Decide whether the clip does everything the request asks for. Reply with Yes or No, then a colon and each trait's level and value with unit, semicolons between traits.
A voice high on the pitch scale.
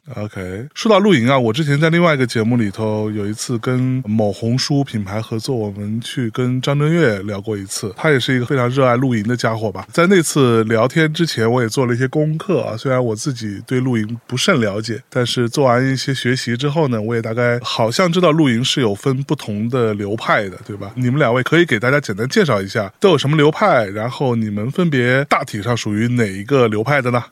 No: low, 125 Hz